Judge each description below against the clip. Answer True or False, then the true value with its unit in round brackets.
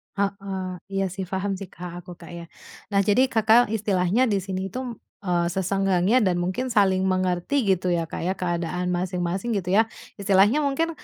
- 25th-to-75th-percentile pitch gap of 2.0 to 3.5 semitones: True (2.4 semitones)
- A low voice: False (190 Hz)